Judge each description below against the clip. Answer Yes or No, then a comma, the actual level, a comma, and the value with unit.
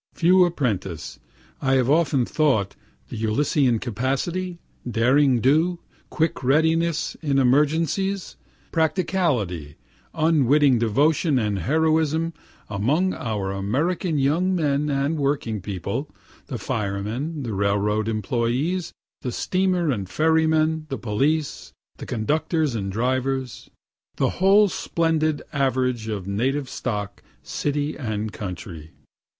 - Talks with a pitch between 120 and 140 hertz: Yes, low, 135 Hz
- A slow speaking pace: Yes, slow, 110 wpm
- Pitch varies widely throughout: Yes, wide, 6.3 semitones